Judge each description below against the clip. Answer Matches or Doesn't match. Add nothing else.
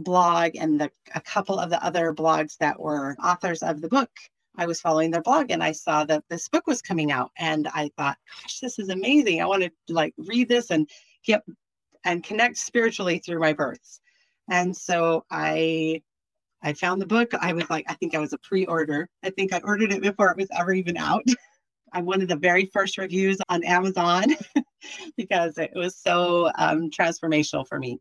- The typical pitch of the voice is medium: Matches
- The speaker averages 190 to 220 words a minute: Matches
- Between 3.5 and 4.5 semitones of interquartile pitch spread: Matches